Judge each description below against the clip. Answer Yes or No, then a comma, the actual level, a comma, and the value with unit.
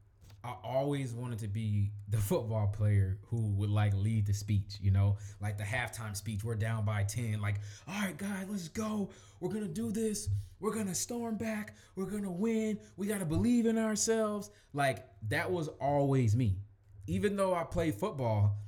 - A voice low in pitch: Yes, low, 115 Hz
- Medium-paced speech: Yes, average, 180 wpm